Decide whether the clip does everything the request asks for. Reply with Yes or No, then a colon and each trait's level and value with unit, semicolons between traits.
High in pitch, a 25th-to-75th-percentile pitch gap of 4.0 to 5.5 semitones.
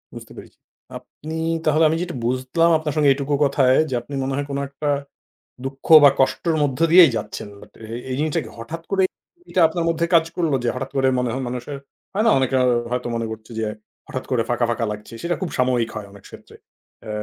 No: low, 135 Hz; average, 4.4 semitones